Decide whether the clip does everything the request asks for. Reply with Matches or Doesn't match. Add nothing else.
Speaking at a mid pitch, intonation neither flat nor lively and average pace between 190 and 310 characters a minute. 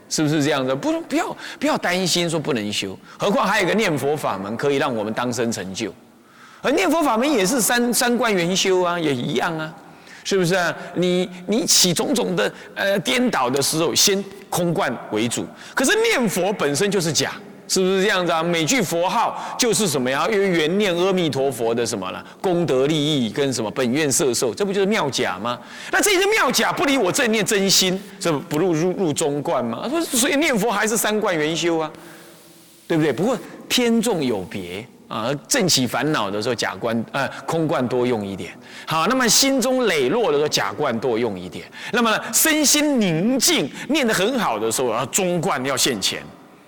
Doesn't match